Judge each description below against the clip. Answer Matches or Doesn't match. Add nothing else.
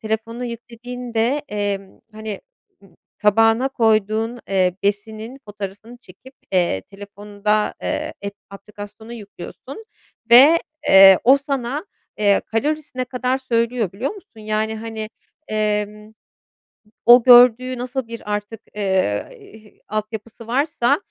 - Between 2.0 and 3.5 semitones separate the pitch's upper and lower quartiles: Matches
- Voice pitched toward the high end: Matches